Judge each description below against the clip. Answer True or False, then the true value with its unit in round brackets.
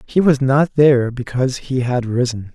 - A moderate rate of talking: True (190 wpm)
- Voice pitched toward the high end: False (130 Hz)